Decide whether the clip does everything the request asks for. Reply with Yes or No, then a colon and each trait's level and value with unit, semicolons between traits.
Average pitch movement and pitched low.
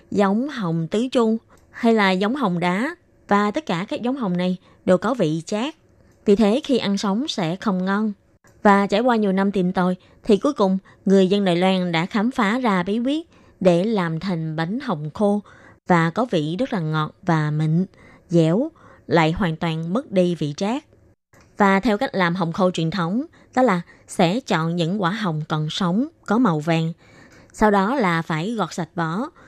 No: average, 4.5 semitones; high, 195 Hz